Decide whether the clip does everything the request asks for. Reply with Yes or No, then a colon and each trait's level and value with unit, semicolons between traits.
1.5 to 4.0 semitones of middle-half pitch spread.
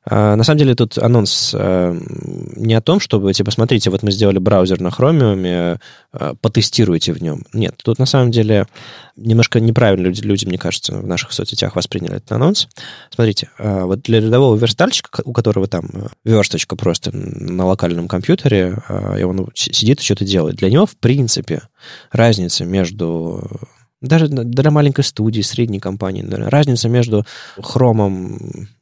No: average, 5.1 semitones